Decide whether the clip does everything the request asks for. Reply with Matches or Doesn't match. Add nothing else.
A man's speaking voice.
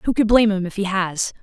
Doesn't match